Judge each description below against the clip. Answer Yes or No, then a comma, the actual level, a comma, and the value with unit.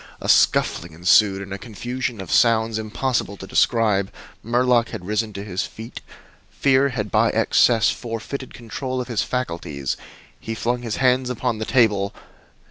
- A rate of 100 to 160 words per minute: Yes, average, 155 wpm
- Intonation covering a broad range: No, average, 3.7 semitones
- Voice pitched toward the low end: Yes, low, 115 Hz